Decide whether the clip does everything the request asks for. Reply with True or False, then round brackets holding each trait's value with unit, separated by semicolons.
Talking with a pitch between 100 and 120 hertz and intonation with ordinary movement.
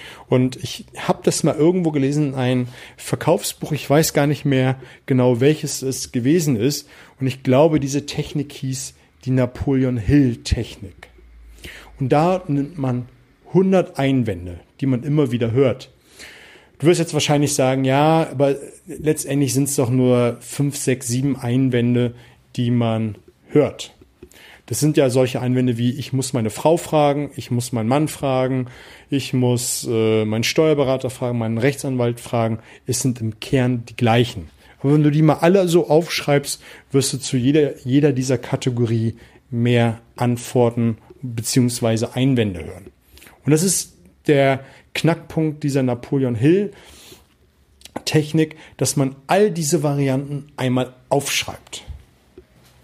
False (130 Hz; 3.1 semitones)